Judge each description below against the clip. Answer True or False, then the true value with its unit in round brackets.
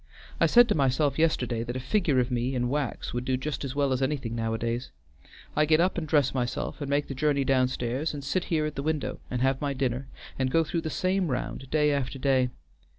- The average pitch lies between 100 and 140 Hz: True (135 Hz)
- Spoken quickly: True (230 wpm)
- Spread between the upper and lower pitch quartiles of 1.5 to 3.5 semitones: True (3.1 semitones)